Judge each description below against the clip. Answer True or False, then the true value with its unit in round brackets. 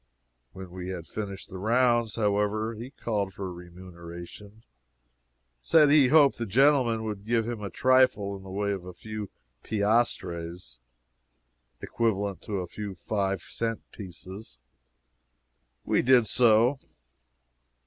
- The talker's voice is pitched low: True (105 Hz)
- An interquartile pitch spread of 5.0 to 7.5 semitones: False (3.6 semitones)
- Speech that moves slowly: True (130 wpm)